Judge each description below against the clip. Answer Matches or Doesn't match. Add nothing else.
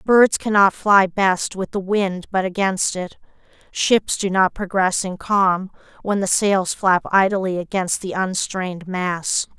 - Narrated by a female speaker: Matches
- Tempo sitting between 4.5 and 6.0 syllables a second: Doesn't match